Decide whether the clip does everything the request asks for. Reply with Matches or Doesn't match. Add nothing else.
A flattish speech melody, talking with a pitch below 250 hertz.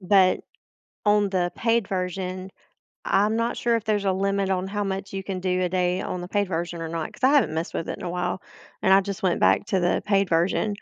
Matches